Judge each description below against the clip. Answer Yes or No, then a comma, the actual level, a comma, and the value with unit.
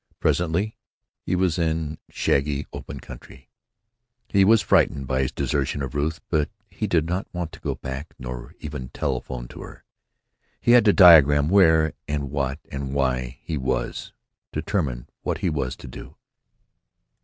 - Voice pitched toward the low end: Yes, very low, 75 Hz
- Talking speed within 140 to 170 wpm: Yes, average, 155 wpm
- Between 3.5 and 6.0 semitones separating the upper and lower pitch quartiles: Yes, average, 4.2 semitones